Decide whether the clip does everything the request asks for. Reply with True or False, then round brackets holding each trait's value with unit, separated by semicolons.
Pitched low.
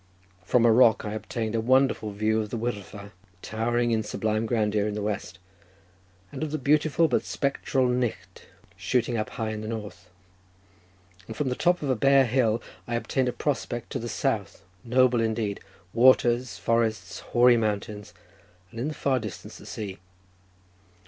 True (115 Hz)